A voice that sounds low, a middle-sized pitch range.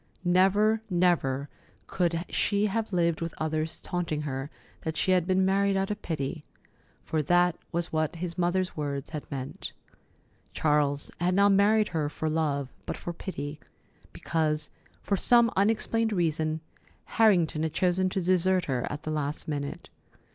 No: medium, 170 Hz; average, 3.6 semitones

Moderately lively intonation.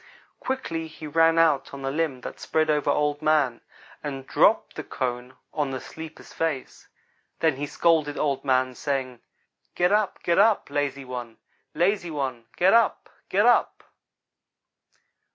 Yes: average, 3.5 semitones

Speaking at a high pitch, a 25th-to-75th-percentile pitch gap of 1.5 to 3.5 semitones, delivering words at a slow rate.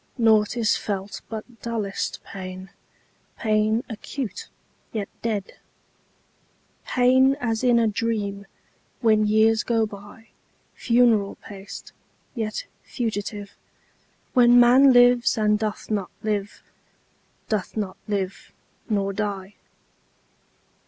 Yes: high, 215 Hz; narrow, 2.5 semitones; slow, 80 wpm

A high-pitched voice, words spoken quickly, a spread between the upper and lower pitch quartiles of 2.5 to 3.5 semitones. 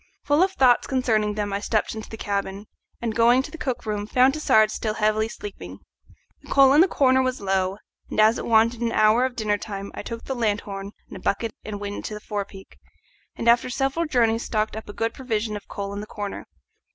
Yes: high, 220 Hz; fast, 225 wpm; average, 3.2 semitones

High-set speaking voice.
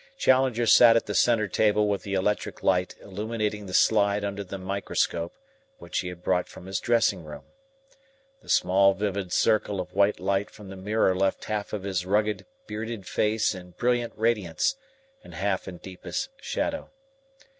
No: low, 100 Hz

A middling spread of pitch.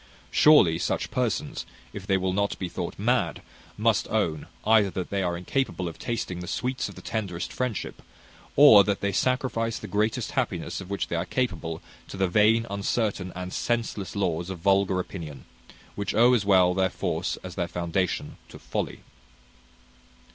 Yes: average, 3.8 semitones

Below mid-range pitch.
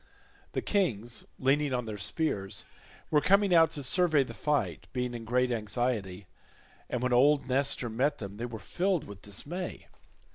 Yes: low, 125 Hz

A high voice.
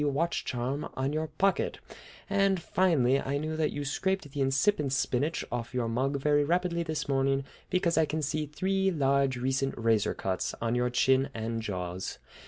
No: medium, 140 Hz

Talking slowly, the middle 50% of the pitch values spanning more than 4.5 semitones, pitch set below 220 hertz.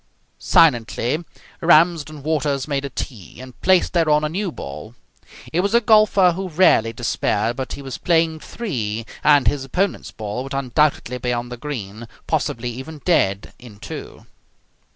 No: average, 155 wpm; wide, 5.6 semitones; medium, 140 Hz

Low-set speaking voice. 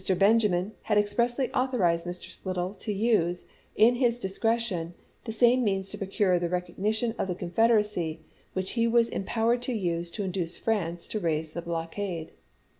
No: high, 195 Hz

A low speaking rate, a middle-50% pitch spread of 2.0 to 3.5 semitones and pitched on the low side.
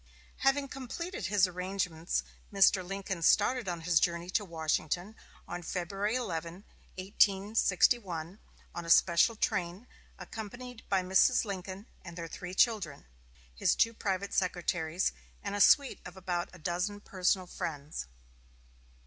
No: slow, 130 wpm; average, 3.0 semitones; medium, 185 Hz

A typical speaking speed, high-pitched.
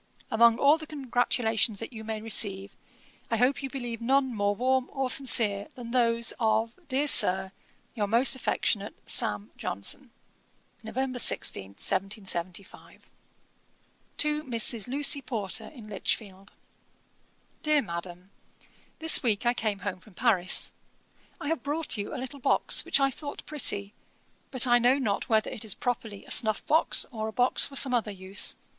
Yes: average, 155 wpm; high, 230 Hz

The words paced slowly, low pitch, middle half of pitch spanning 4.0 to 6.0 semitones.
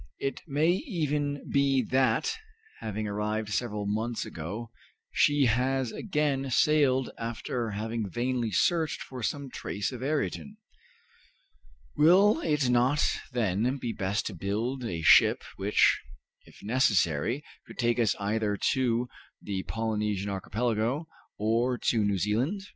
Yes: slow, 125 wpm; low, 120 Hz; average, 4.6 semitones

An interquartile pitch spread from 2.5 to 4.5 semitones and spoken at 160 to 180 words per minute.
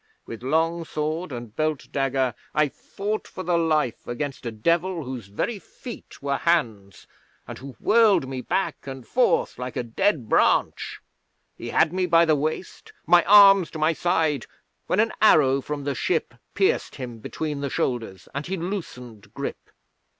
No: average, 5.3 semitones; average, 165 wpm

